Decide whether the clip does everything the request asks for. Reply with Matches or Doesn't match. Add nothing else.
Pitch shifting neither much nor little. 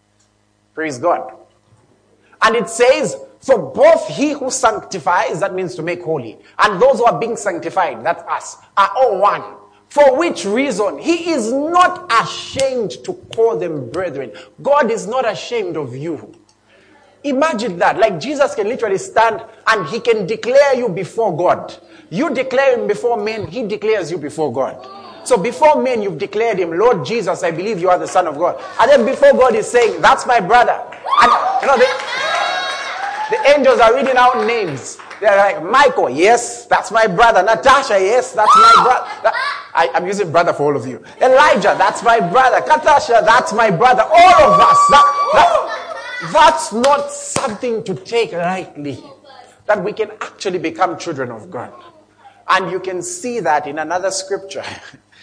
Doesn't match